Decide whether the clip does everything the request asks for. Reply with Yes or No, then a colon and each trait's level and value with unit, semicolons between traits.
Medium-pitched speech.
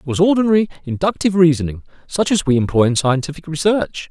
Yes: medium, 160 Hz